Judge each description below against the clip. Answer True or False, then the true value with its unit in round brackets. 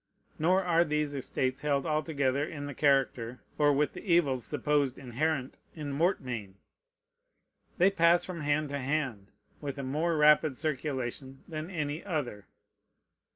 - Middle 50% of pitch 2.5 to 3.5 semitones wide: True (2.9 semitones)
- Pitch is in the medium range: True (145 Hz)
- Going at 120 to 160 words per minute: True (140 wpm)